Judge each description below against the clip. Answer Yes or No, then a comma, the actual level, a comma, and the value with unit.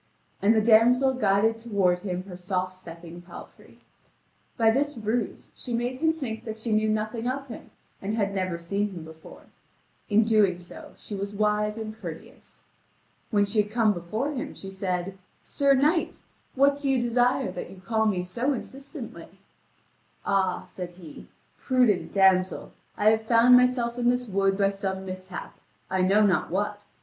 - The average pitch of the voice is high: Yes, high, 210 Hz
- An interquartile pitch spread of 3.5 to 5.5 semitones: Yes, average, 4.0 semitones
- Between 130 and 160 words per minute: No, average, 170 wpm